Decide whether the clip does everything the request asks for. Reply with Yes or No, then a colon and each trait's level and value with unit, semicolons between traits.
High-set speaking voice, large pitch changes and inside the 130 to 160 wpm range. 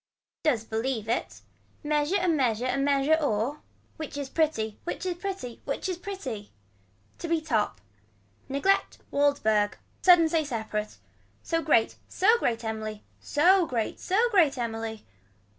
Yes: very high, 280 Hz; wide, 6.8 semitones; average, 140 wpm